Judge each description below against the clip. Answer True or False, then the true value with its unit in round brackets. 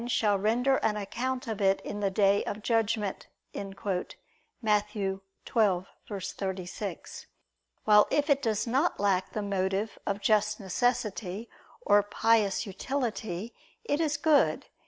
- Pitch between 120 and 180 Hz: False (210 Hz)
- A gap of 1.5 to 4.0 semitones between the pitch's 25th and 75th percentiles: True (2.9 semitones)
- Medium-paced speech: False (120 wpm)